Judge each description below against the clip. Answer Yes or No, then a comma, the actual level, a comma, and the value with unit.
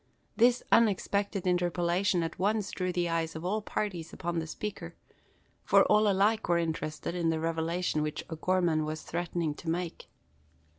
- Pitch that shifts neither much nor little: Yes, average, 3.1 semitones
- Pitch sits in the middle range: Yes, medium, 175 Hz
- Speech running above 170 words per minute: No, average, 155 wpm